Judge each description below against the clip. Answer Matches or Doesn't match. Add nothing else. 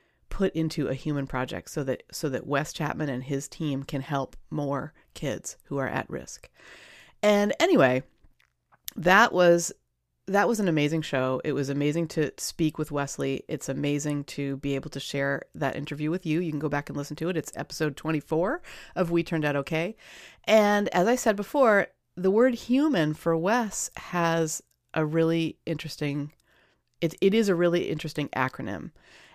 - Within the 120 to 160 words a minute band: Doesn't match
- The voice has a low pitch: Doesn't match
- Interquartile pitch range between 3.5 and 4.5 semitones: Matches